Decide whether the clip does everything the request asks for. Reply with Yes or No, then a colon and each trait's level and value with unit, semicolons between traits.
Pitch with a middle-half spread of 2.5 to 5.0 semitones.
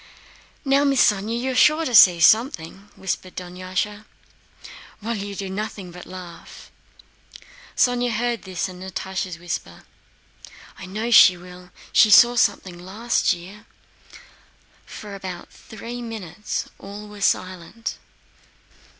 Yes: average, 3.9 semitones